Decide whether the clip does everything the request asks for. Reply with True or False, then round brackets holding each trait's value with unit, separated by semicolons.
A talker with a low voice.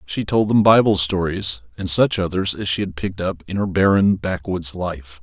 True (90 Hz)